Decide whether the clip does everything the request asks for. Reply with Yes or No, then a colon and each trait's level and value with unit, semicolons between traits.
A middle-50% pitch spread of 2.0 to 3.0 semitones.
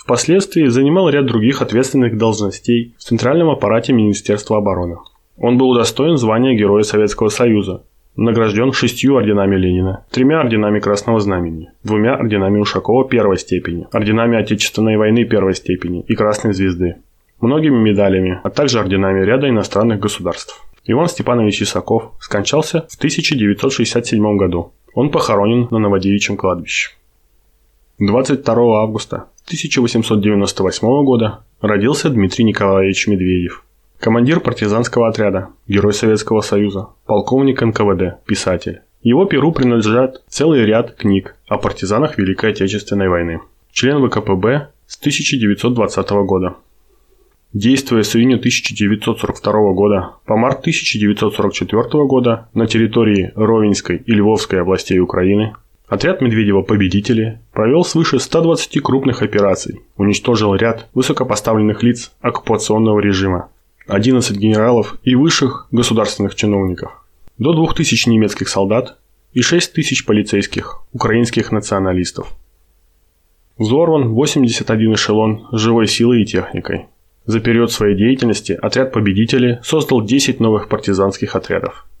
No: average, 3.5 semitones